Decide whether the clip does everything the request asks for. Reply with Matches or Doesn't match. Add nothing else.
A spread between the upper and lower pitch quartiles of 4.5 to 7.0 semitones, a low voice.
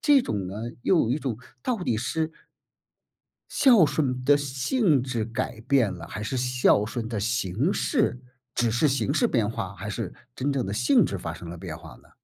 Matches